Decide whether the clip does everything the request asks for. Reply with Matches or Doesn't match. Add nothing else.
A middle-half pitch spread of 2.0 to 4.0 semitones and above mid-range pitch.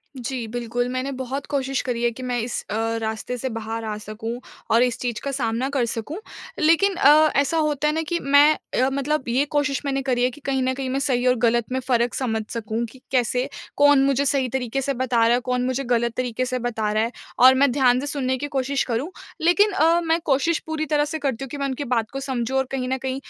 Matches